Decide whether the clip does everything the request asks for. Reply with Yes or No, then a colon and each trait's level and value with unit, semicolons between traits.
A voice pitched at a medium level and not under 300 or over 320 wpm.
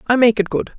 No: high, 220 Hz; fast, 305 wpm